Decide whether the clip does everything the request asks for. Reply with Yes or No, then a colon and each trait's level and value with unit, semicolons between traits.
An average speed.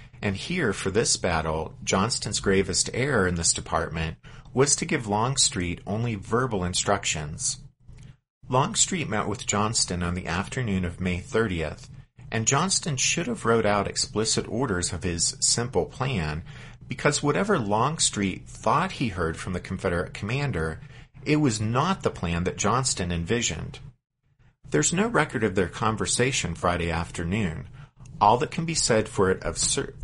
Yes: average, 150 wpm